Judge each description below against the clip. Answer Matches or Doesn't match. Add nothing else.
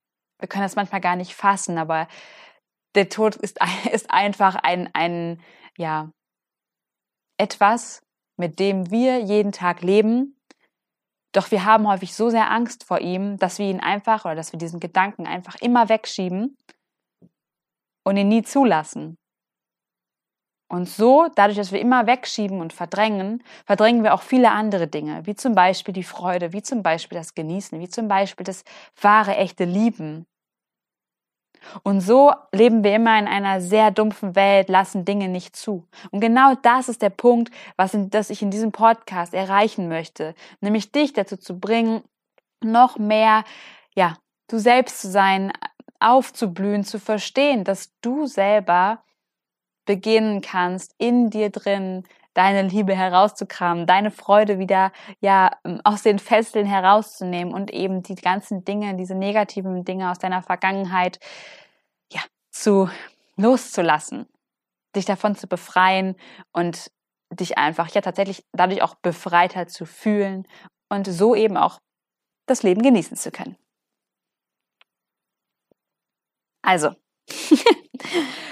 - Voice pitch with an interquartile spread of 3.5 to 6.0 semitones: Doesn't match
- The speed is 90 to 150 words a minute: Matches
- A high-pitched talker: Matches